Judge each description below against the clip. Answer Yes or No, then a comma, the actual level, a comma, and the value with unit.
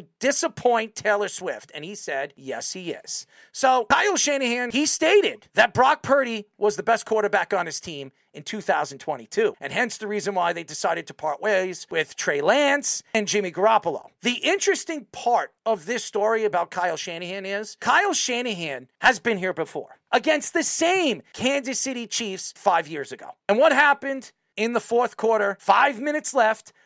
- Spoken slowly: No, average, 170 wpm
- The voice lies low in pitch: No, high, 225 Hz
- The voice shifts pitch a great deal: Yes, wide, 5.9 semitones